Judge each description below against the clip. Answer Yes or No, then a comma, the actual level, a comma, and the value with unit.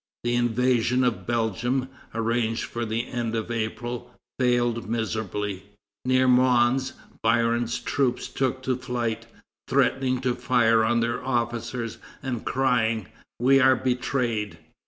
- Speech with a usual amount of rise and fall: No, narrow, 1.8 semitones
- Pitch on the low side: Yes, low, 120 Hz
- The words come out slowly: Yes, slow, 120 wpm